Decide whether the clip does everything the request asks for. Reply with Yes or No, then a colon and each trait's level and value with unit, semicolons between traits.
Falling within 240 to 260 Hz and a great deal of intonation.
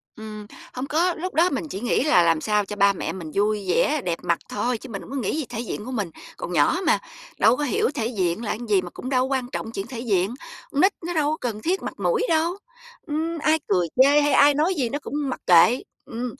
Yes: high, 245 Hz; wide, 6.3 semitones